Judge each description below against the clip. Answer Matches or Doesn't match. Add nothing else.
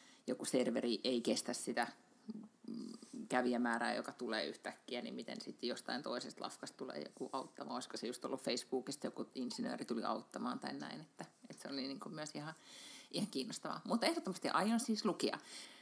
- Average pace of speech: Doesn't match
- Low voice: Doesn't match